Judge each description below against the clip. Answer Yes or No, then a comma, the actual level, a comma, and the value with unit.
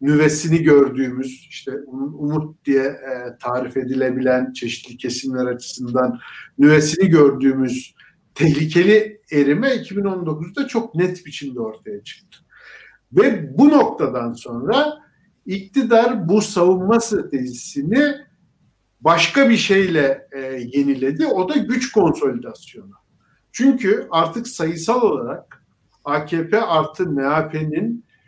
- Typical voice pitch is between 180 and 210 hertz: No, medium, 155 Hz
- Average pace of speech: No, slow, 90 wpm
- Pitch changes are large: Yes, wide, 7.2 semitones